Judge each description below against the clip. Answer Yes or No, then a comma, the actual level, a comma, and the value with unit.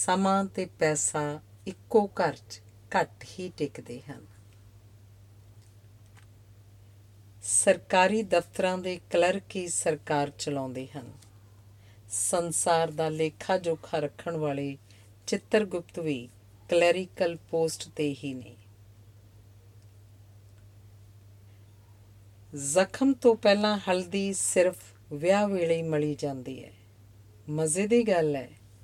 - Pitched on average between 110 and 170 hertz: Yes, medium, 140 Hz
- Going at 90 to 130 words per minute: Yes, average, 100 wpm